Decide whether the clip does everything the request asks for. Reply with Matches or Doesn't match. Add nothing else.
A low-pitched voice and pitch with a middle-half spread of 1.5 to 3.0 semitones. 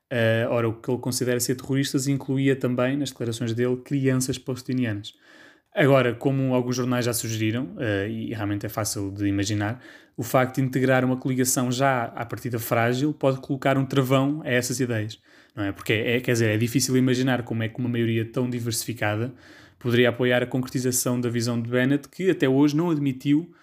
Matches